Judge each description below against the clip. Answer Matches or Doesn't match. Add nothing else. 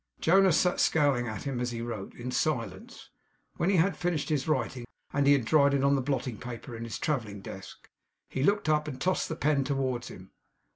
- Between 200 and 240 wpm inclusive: Matches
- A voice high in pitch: Doesn't match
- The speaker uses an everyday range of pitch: Matches